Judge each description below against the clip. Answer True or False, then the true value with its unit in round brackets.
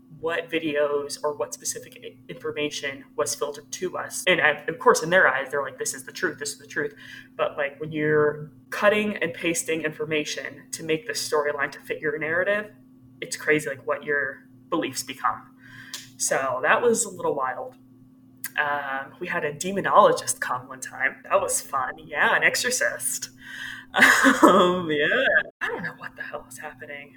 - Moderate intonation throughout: True (4.0 semitones)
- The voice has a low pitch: False (150 Hz)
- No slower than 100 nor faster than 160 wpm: False (175 wpm)